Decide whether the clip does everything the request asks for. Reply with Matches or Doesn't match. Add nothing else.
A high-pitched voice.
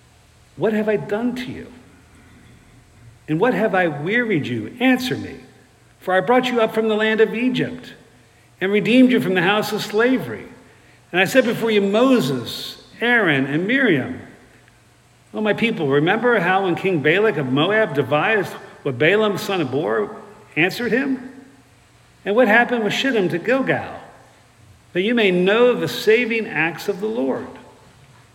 Matches